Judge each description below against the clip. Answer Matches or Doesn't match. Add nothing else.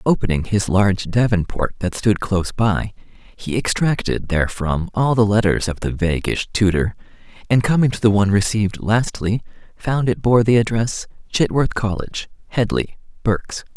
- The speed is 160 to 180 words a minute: Doesn't match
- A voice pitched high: Doesn't match